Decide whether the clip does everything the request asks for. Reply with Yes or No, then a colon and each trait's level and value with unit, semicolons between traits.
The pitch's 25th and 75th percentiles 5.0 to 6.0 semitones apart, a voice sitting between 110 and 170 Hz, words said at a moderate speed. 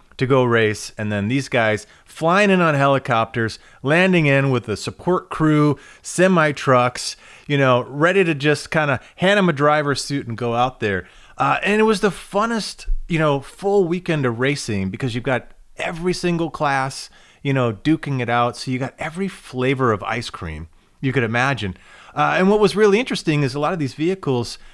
Yes: wide, 5.6 semitones; medium, 140 Hz; average, 195 wpm